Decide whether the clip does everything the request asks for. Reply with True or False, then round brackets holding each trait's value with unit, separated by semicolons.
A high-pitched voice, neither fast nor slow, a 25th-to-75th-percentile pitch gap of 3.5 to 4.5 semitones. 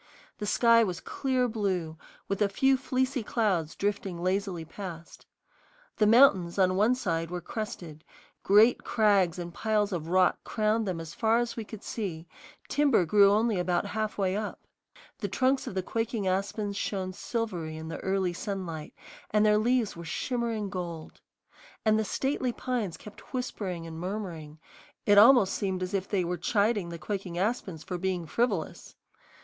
True (200 Hz; 165 wpm; 3.8 semitones)